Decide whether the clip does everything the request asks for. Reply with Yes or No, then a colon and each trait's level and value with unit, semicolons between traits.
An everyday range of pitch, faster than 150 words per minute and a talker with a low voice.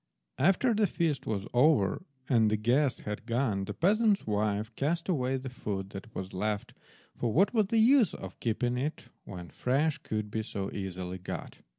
No: wide, 7.4 semitones; average, 180 wpm; low, 120 Hz